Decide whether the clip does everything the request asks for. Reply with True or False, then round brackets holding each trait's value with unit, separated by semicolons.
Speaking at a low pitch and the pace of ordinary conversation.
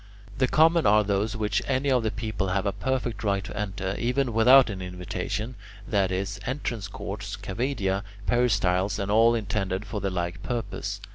True (105 Hz; 170 wpm)